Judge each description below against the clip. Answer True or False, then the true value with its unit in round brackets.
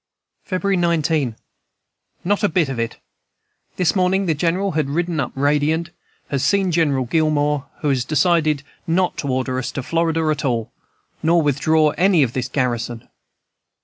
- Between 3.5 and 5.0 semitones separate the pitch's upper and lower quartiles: True (4.0 semitones)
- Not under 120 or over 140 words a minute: False (155 wpm)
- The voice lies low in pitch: False (155 Hz)